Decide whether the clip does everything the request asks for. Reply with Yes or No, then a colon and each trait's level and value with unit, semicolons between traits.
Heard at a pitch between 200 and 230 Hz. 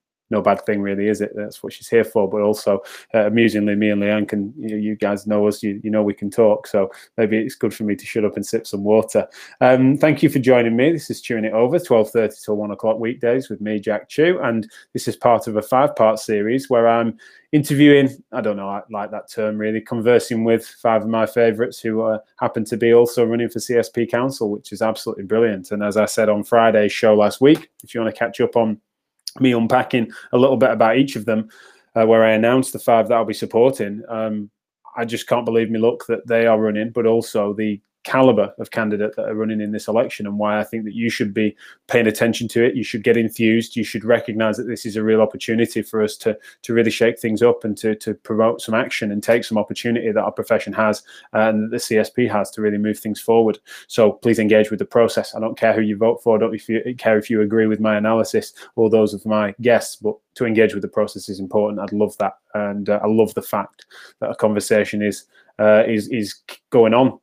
No: low, 110 Hz